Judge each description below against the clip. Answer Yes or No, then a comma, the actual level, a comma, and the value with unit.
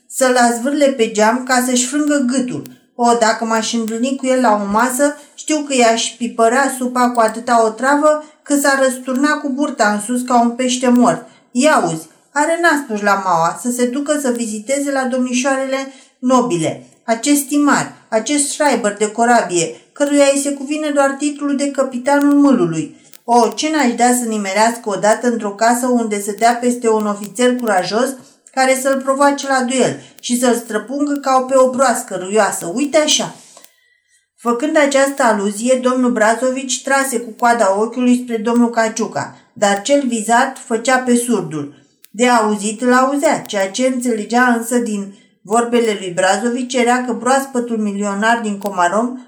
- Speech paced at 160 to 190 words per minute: Yes, average, 165 wpm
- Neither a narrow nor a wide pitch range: Yes, average, 3.3 semitones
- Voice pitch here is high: Yes, high, 245 Hz